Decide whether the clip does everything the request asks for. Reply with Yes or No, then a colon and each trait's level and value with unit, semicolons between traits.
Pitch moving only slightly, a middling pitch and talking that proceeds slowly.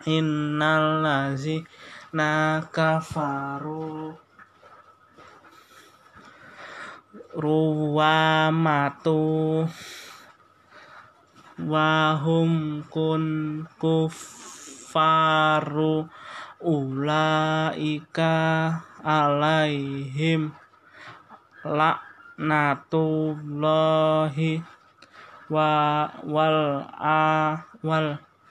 Yes: narrow, 0.7 semitones; medium, 155 Hz; slow, 35 wpm